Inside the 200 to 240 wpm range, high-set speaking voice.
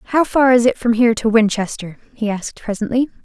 Yes: fast, 205 wpm; high, 230 Hz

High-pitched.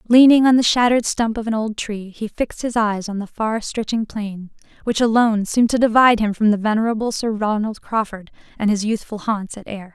Yes: high, 220 Hz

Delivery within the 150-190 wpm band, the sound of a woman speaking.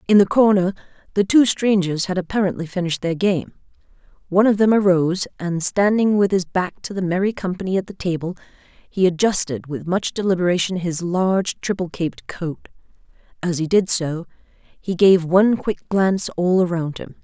Yes: average, 170 wpm; female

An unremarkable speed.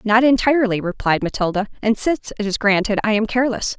Yes: average, 190 wpm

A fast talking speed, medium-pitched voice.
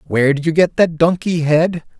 Yes: fast, 210 wpm; medium, 165 Hz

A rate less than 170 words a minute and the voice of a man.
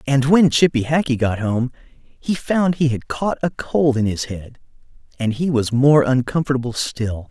No: average, 180 wpm; male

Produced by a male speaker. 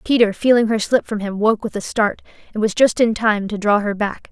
No: female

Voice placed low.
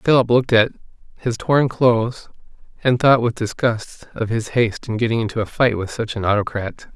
Yes: low, 115 Hz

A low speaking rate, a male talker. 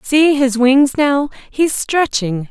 No: slow, 120 wpm; female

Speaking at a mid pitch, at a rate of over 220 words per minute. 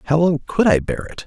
Yes: medium, 155 Hz; fast, 285 wpm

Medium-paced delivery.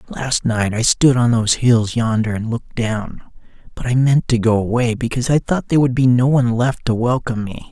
No: fast, 225 wpm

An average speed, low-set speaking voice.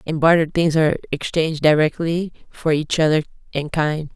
No: average, 160 wpm; medium, 155 Hz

